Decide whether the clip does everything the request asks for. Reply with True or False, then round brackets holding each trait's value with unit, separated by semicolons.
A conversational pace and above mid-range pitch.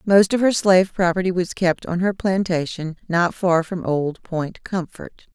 False (180 wpm; 180 Hz)